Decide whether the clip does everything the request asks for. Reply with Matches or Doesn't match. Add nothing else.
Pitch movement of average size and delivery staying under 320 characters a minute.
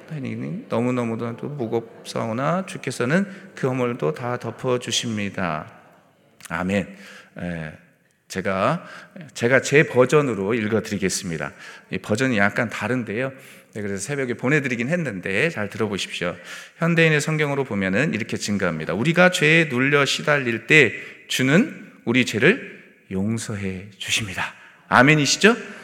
Matches